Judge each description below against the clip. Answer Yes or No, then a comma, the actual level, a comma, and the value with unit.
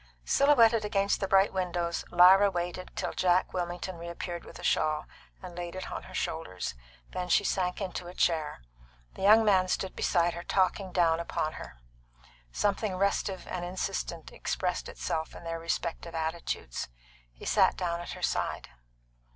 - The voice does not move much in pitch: Yes, narrow, 2.1 semitones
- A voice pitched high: No, medium, 180 Hz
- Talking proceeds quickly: No, average, 160 wpm